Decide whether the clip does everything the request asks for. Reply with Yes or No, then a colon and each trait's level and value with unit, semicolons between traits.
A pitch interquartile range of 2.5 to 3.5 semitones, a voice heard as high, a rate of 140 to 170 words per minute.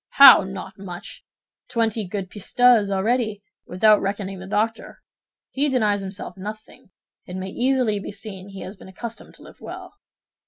Yes: average, 2.9 semitones; high, 205 Hz; average, 155 wpm